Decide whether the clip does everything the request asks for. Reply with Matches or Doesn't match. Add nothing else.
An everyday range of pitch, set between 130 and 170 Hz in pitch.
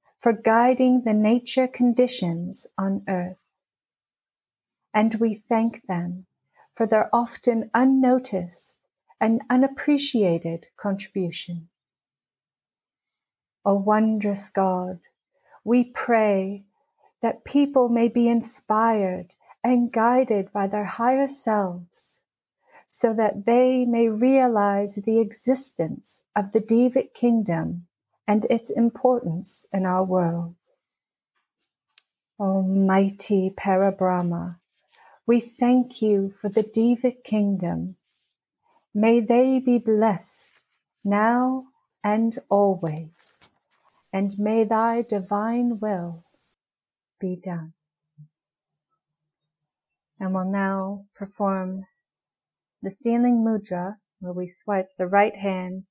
Doesn't match